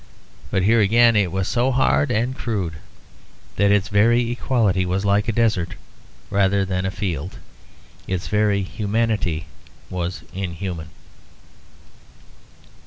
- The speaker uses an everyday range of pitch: Yes, average, 3.6 semitones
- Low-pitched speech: Yes, low, 100 Hz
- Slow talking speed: Yes, slow, 120 wpm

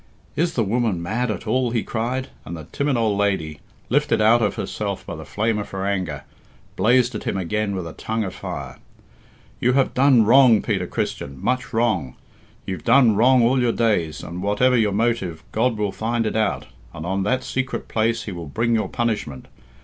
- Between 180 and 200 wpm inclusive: Yes, average, 195 wpm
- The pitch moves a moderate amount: Yes, average, 4.1 semitones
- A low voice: Yes, low, 110 Hz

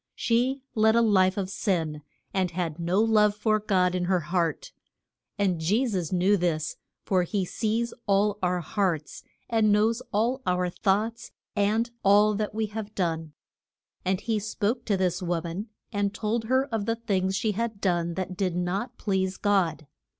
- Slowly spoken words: No, average, 170 wpm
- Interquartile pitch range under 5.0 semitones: Yes, average, 3.3 semitones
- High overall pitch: Yes, high, 200 Hz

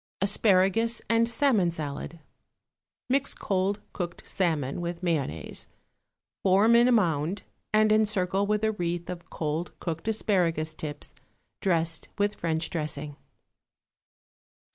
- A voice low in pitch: No, medium, 180 Hz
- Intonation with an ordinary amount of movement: Yes, average, 4.5 semitones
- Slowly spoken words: Yes, slow, 115 wpm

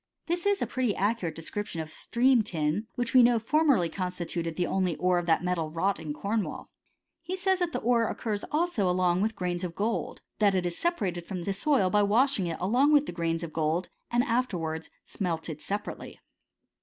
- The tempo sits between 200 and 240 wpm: Yes, fast, 205 wpm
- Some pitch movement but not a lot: No, wide, 5.8 semitones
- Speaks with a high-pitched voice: Yes, high, 195 Hz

